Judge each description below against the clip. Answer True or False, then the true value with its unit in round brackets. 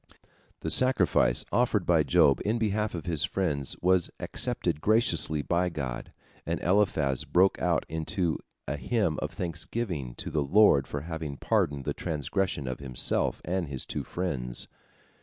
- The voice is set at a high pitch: False (80 Hz)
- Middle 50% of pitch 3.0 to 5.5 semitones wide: True (5.2 semitones)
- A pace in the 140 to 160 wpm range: True (150 wpm)